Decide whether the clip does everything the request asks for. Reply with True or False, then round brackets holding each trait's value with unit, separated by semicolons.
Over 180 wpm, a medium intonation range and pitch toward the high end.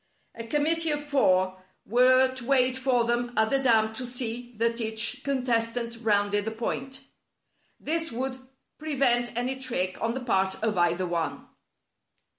False (155 wpm; 3.0 semitones; 240 Hz)